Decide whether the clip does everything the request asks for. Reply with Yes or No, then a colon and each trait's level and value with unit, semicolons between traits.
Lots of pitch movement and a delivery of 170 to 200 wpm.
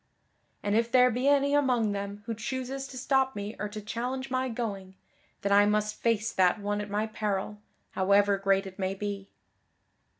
No: average, 3.8 semitones; average, 180 wpm